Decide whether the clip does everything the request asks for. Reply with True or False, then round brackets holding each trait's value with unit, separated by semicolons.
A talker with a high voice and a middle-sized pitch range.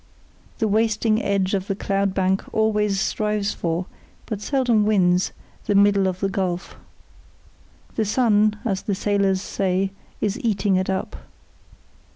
False (200 Hz; 1.9 semitones)